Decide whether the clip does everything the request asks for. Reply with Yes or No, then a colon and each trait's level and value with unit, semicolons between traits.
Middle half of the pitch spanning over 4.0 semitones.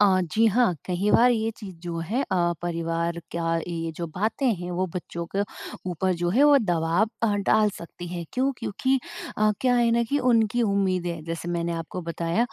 Yes: average, 4.9 semitones